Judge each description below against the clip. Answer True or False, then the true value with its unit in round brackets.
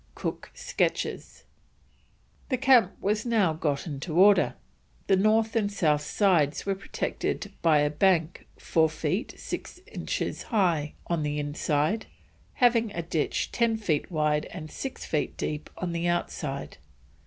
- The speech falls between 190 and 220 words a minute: False (140 wpm)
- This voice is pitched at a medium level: True (175 Hz)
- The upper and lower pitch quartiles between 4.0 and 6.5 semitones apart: True (5.4 semitones)